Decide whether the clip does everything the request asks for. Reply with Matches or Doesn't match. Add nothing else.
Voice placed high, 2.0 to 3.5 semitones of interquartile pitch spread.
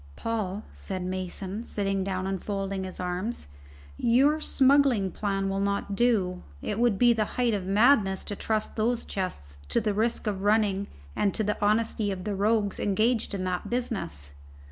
Matches